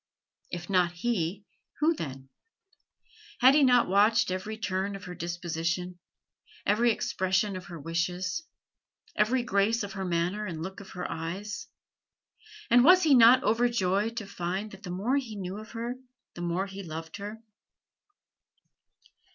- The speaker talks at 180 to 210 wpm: No, average, 150 wpm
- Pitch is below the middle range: No, high, 195 Hz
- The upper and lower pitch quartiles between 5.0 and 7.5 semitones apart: No, average, 4.2 semitones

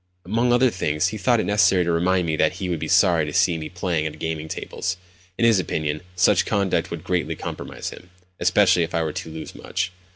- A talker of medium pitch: No, very low, 90 Hz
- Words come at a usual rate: No, fast, 225 wpm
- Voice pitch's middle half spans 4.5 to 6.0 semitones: No, average, 2.8 semitones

